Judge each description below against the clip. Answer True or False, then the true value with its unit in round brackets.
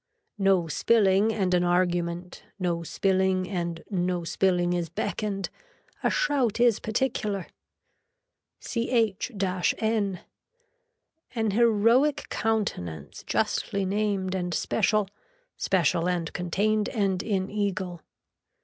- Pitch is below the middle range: False (190 Hz)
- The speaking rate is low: True (100 wpm)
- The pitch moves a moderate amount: True (3.3 semitones)